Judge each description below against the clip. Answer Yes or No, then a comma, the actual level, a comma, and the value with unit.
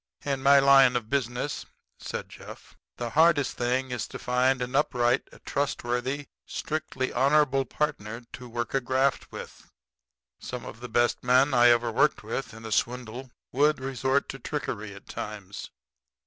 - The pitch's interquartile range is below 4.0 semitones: Yes, narrow, 2.4 semitones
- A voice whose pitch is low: Yes, low, 125 Hz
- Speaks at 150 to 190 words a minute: Yes, average, 155 wpm